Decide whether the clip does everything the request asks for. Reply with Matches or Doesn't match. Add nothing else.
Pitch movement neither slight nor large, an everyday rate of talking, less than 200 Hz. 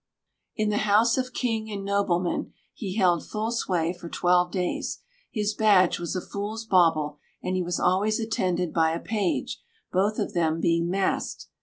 Matches